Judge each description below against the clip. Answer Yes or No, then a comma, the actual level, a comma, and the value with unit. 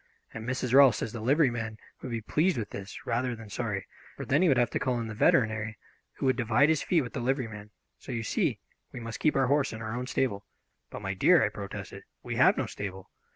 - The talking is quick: Yes, fast, 240 wpm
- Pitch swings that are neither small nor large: Yes, average, 3.3 semitones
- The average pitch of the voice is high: No, low, 120 Hz